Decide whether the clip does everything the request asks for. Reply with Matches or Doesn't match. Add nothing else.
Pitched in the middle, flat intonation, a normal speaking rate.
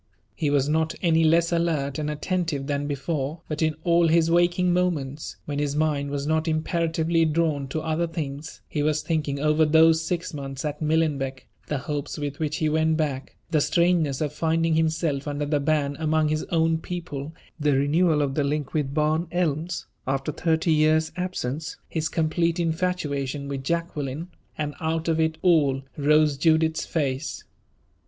Matches